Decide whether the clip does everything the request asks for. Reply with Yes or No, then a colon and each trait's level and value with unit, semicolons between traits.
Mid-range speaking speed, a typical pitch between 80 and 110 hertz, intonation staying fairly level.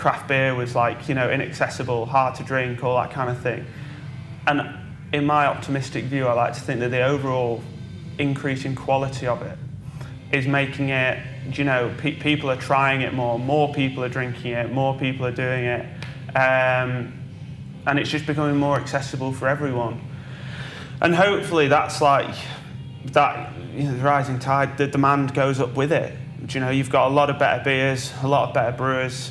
No: average, 190 wpm; low, 135 Hz; narrow, 1.7 semitones